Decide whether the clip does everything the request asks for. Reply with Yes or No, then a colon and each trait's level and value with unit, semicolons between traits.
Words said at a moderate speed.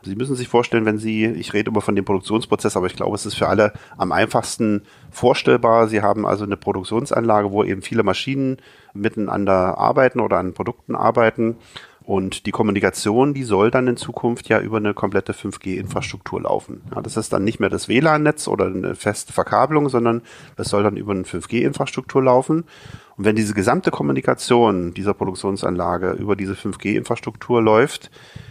Yes: average, 170 wpm